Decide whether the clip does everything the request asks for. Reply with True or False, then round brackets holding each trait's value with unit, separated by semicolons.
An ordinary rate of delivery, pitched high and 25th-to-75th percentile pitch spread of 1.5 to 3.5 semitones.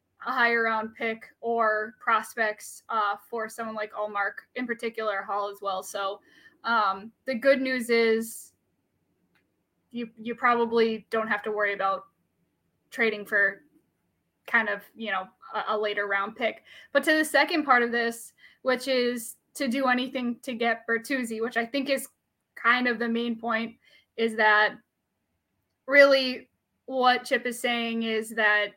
True (155 wpm; 230 Hz; 2.7 semitones)